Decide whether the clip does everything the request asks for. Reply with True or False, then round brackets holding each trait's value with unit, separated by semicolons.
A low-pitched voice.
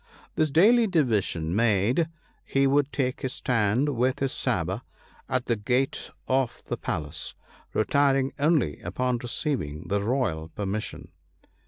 True (125 Hz)